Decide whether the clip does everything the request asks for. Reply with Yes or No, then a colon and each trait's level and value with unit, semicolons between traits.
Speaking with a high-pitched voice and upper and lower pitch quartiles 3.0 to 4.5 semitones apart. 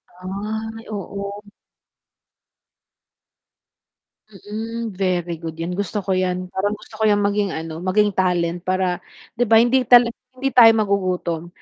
Yes: high, 200 Hz; average, 3.3 semitones